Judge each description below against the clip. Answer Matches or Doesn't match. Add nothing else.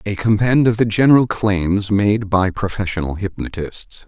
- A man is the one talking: Matches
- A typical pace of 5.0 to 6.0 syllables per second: Doesn't match